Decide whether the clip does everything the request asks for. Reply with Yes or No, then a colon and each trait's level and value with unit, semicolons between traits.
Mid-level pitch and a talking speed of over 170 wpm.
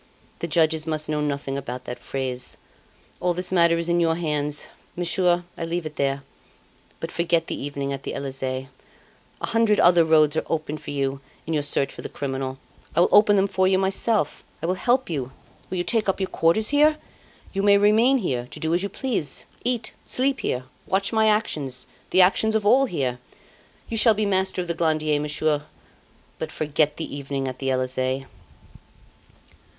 Yes: medium, 165 Hz; average, 190 wpm